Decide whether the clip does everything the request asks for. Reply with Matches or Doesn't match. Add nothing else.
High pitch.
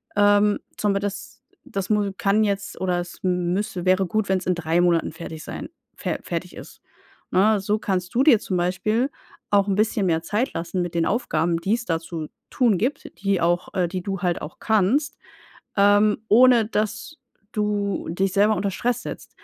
Matches